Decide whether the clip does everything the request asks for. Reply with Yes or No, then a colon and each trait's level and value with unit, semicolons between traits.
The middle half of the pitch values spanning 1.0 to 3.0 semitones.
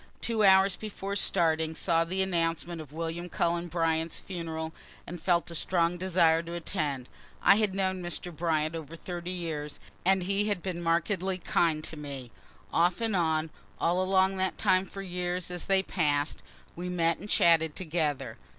Yes: narrow, 2.5 semitones